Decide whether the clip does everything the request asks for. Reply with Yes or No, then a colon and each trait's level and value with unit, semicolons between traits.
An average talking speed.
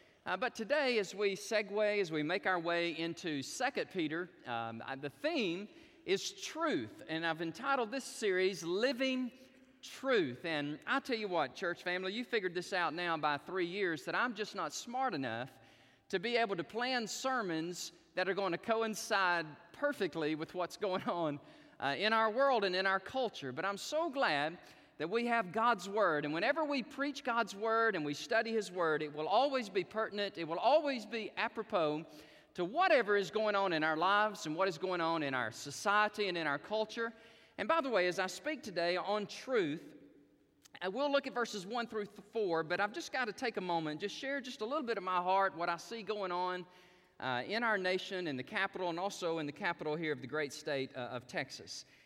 No: fast, 210 wpm